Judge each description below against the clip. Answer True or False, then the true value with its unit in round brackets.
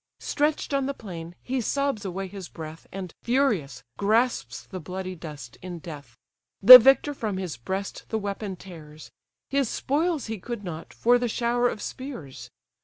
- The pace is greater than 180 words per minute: False (165 wpm)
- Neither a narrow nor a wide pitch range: False (6.6 semitones)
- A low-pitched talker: False (200 Hz)